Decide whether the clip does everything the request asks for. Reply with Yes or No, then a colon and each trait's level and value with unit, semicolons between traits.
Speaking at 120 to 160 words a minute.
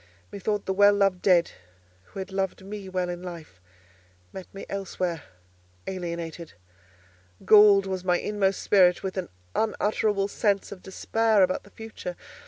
Yes: average, 145 wpm